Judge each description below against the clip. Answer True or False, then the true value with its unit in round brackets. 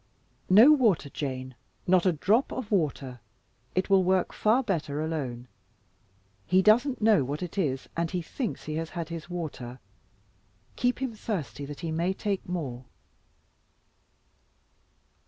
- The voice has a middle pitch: True (175 Hz)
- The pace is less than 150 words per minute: True (140 wpm)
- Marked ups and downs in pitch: True (5.8 semitones)